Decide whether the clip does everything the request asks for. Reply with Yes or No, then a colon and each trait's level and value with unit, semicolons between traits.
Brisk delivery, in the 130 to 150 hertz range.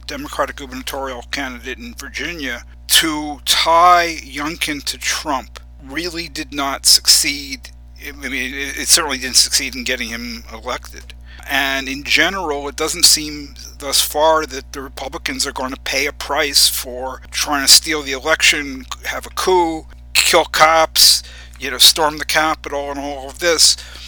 No: average, 150 wpm; low, 135 Hz